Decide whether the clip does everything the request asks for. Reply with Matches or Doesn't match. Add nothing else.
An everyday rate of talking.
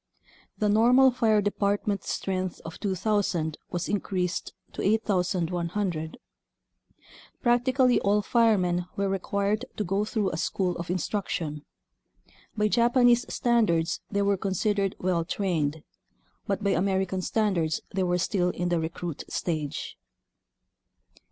Doesn't match